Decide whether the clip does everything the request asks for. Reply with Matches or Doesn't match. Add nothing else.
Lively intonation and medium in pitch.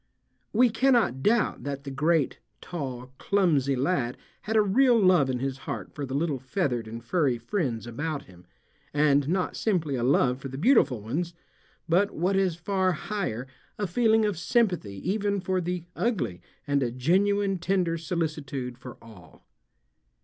Matches